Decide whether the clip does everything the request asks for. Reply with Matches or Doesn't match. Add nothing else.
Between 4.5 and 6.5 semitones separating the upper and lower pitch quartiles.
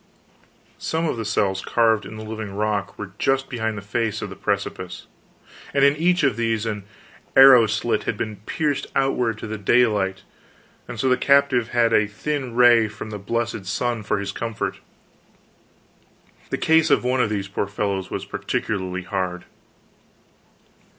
Doesn't match